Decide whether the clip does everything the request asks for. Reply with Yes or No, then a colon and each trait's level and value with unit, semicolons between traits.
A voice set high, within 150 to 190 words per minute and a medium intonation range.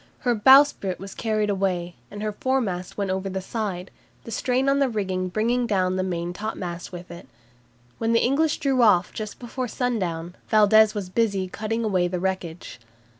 Yes: high, 205 Hz; average, 175 wpm; average, 3.9 semitones